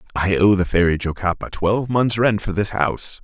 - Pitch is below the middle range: Yes, low, 100 Hz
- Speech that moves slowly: No, fast, 205 wpm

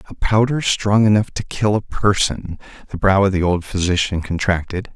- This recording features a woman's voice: No, male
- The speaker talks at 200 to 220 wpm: No, average, 180 wpm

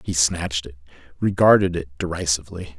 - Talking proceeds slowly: Yes, slow, 130 wpm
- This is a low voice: Yes, very low, 80 Hz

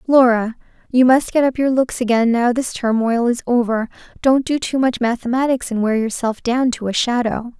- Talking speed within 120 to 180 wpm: No, average, 195 wpm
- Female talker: Yes, female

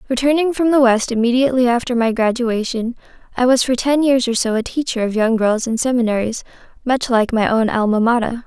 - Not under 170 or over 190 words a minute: No, average, 200 wpm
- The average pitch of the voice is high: Yes, high, 240 Hz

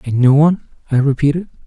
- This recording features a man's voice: Yes, male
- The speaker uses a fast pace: No, average, 180 wpm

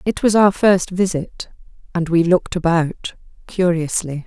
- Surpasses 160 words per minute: No, average, 140 wpm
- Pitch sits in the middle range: Yes, medium, 175 Hz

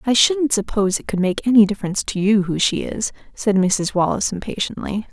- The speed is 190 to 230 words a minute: Yes, average, 200 wpm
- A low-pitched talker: No, high, 210 Hz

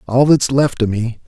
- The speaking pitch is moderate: No, low, 125 Hz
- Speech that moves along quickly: Yes, fast, 235 wpm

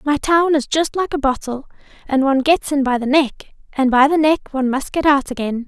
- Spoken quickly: Yes, fast, 245 wpm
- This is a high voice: Yes, very high, 280 Hz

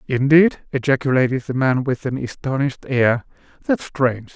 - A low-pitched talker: Yes, low, 130 Hz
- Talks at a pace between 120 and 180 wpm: Yes, average, 140 wpm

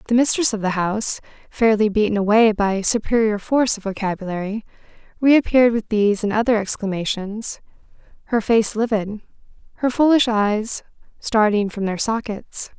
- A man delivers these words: No, female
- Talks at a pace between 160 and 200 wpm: No, slow, 135 wpm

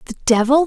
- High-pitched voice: Yes, very high, 265 Hz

